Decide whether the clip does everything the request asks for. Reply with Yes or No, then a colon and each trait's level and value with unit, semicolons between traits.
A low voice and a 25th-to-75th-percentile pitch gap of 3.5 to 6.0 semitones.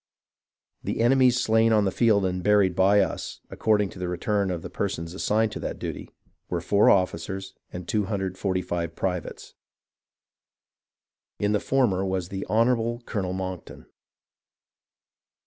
No: very low, 95 Hz; average, 2.9 semitones